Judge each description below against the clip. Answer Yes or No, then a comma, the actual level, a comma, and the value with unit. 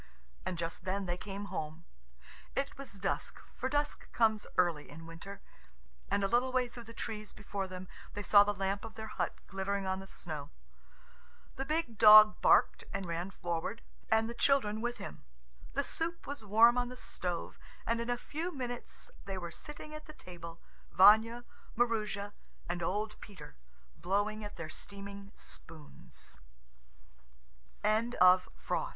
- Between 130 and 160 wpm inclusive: Yes, average, 155 wpm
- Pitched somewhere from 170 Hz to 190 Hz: No, high, 205 Hz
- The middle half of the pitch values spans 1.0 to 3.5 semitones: No, average, 4.2 semitones